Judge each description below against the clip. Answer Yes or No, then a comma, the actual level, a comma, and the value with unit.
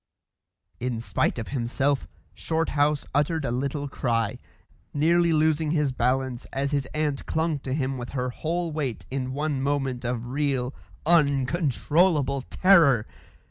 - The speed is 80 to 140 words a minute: Yes, slow, 135 wpm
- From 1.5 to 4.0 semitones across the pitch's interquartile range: Yes, average, 3.3 semitones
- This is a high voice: No, medium, 140 Hz